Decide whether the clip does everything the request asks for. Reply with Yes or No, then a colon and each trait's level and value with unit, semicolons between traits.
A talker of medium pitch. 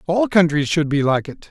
Yes: medium, 160 Hz